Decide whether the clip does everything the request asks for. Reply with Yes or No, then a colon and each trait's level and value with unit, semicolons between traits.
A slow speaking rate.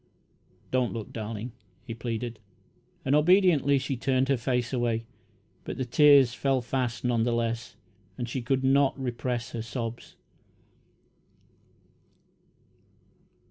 Yes: slow, 120 wpm